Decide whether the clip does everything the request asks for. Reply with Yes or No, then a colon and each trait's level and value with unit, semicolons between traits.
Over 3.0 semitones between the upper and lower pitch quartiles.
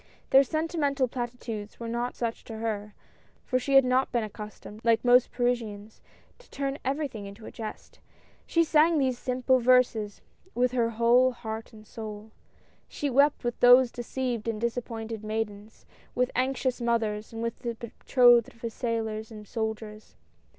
No: narrow, 2.5 semitones